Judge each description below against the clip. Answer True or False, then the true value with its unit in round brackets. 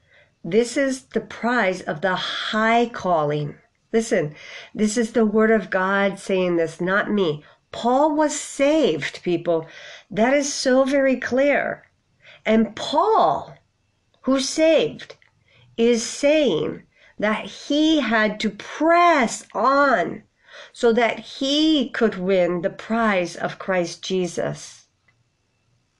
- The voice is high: True (220 Hz)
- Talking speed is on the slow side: True (115 wpm)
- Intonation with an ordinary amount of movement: False (6.6 semitones)